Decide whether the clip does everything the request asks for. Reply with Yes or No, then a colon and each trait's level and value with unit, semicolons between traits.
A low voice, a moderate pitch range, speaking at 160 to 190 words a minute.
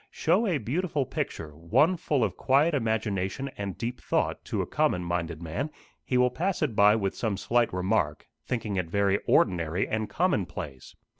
No: low, 110 Hz; wide, 6.9 semitones; average, 170 wpm